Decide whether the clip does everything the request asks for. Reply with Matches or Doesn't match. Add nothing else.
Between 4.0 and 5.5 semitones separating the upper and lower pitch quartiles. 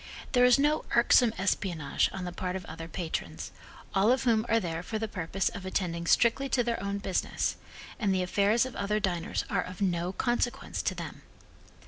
Matches